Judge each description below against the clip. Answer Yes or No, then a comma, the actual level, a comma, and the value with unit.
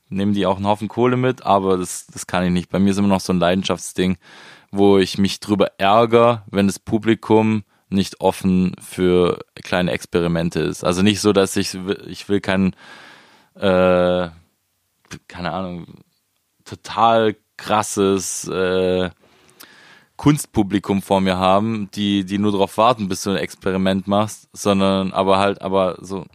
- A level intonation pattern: Yes, narrow, 1.8 semitones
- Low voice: Yes, very low, 95 Hz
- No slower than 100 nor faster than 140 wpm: No, average, 155 wpm